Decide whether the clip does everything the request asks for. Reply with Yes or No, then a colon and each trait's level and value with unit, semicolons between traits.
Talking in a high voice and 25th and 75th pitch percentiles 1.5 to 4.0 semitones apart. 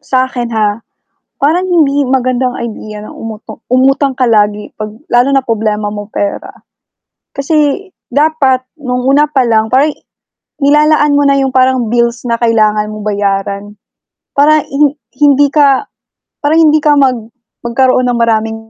No: very high, 255 Hz; average, 4.4 semitones